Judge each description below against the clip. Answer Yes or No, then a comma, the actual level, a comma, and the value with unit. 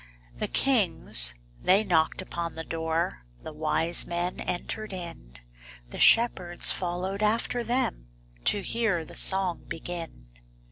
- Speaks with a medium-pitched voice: Yes, medium, 175 Hz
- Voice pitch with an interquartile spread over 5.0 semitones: No, average, 3.7 semitones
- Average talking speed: No, slow, 125 wpm